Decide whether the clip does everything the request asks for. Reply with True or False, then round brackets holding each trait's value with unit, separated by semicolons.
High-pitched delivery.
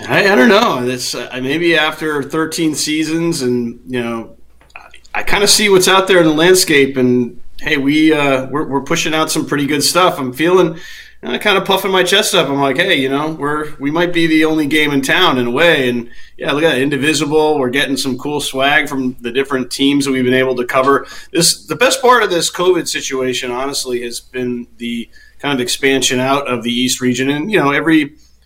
False (140 Hz)